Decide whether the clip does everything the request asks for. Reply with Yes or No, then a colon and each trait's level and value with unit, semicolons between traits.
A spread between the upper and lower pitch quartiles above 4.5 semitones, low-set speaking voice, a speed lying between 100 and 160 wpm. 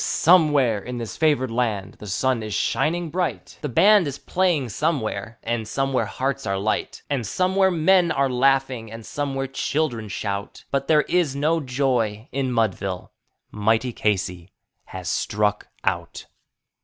Yes: wide, 5.5 semitones; low, 130 Hz; average, 145 wpm